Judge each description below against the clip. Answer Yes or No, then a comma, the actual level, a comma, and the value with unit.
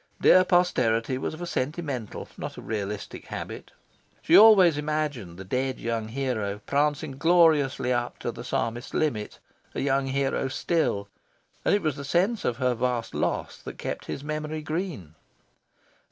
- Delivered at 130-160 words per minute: Yes, average, 155 wpm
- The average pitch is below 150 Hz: Yes, low, 135 Hz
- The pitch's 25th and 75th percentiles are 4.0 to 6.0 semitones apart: Yes, average, 4.9 semitones